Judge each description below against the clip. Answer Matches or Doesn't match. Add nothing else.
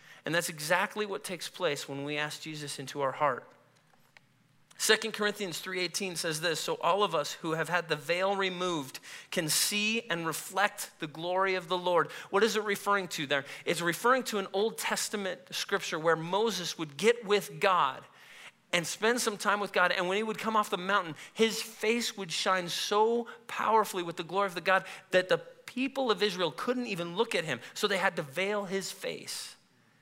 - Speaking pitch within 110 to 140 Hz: Doesn't match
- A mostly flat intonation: Doesn't match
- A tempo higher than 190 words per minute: Matches